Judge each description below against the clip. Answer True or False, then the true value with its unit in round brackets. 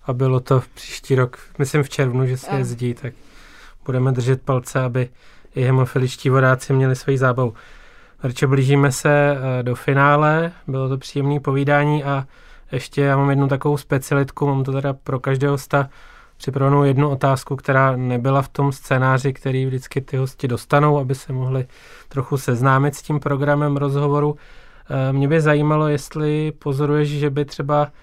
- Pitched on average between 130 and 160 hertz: True (140 Hz)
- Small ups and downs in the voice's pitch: True (1.6 semitones)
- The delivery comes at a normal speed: True (160 wpm)